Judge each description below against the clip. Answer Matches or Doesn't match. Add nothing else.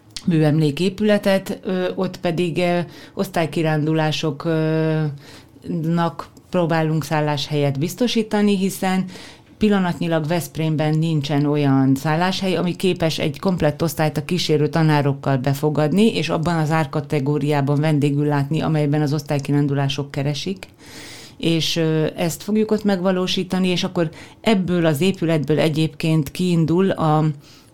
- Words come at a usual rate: Doesn't match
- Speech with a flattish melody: Doesn't match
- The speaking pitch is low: Doesn't match